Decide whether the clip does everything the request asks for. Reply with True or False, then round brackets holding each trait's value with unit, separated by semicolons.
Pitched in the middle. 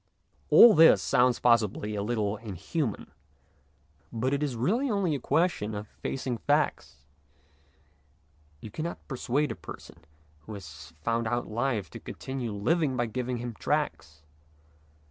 False (120 Hz)